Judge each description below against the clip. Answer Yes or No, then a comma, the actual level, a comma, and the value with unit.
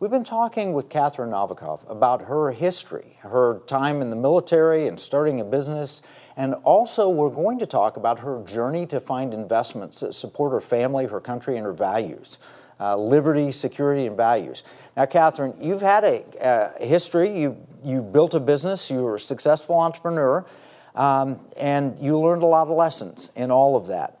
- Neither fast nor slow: Yes, average, 180 wpm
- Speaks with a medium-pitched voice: Yes, medium, 145 Hz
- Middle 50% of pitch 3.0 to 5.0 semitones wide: Yes, average, 4.3 semitones